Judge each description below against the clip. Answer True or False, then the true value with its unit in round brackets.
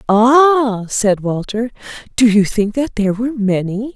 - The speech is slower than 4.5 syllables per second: True (4.2 syllables/s)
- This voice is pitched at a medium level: False (225 Hz)